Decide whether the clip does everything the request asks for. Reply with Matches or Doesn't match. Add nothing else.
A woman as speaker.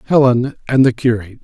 Doesn't match